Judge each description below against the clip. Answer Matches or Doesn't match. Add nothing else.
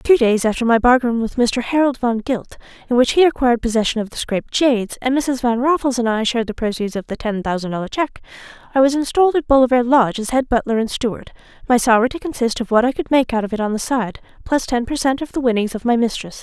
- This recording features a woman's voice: Matches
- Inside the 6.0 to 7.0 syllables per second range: Matches